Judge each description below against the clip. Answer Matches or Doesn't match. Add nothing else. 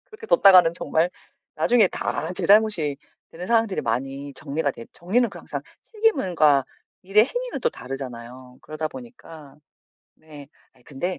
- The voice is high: Doesn't match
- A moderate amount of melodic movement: Doesn't match